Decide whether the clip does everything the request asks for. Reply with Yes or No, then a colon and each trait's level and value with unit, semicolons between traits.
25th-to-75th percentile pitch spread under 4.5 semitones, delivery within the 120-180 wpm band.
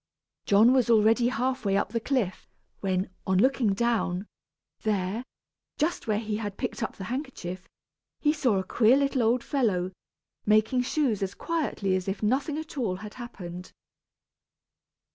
No: average, 4.8 semitones; average, 155 wpm